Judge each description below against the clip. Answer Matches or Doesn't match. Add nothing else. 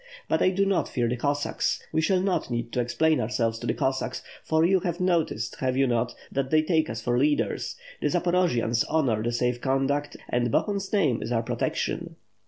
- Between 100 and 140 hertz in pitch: Matches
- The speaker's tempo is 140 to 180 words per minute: Doesn't match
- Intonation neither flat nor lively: Doesn't match